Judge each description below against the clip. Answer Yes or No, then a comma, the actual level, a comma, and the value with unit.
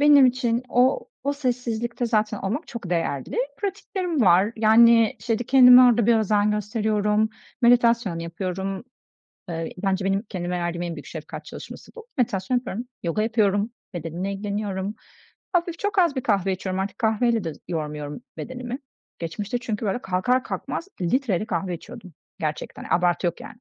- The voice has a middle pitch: No, high, 215 Hz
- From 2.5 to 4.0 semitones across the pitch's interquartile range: No, average, 4.7 semitones